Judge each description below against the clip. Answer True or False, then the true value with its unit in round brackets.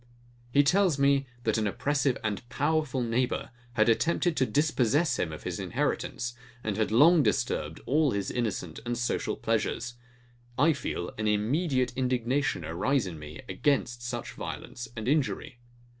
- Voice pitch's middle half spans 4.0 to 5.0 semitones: True (4.5 semitones)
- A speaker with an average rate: True (150 wpm)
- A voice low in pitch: True (125 Hz)